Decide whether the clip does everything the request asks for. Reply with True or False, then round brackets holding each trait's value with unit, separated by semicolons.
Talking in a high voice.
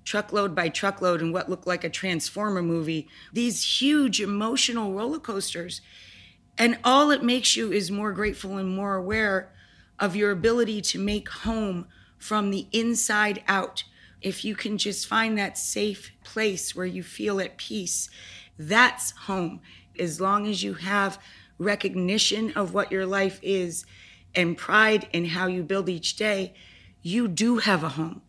True (195 Hz)